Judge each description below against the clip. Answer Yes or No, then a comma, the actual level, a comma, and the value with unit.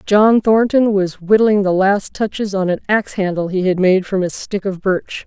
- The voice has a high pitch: Yes, high, 195 Hz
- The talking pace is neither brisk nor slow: No, fast, 215 wpm